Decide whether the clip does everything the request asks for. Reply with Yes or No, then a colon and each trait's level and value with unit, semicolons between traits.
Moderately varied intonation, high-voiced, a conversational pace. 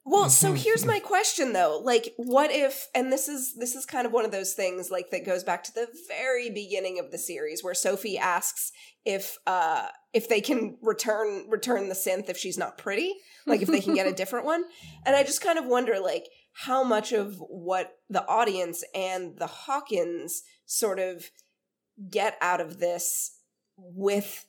No: wide, 7.0 semitones; high, 225 Hz; average, 190 wpm